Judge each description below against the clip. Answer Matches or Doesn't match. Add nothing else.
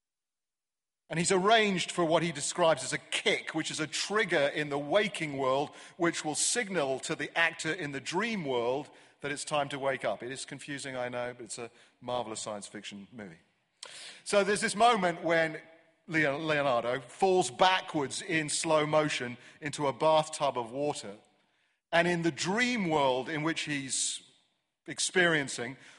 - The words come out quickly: Doesn't match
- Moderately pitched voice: Matches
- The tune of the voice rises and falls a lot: Doesn't match